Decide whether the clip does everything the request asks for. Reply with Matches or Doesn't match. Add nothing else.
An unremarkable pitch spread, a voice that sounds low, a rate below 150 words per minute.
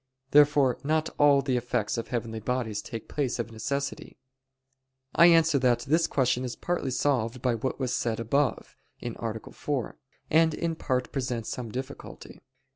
Doesn't match